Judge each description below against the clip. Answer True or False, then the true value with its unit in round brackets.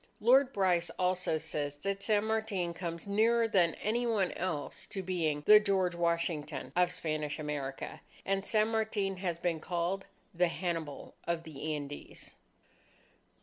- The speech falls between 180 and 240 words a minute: False (145 wpm)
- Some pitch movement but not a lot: True (3.7 semitones)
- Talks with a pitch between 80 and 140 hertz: False (180 Hz)